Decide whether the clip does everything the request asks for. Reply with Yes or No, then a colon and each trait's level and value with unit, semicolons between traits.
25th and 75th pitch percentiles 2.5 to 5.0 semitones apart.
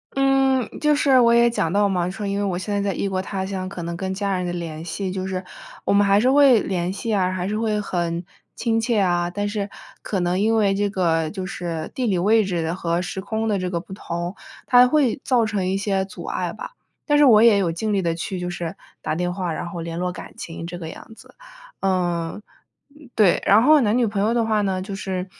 Yes: average, 3.6 semitones